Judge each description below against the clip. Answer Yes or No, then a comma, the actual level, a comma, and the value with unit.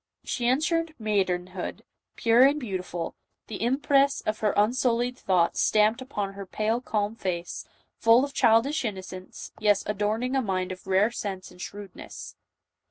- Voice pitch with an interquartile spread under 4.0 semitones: No, average, 4.4 semitones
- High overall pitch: Yes, high, 215 Hz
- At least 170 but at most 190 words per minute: No, average, 145 wpm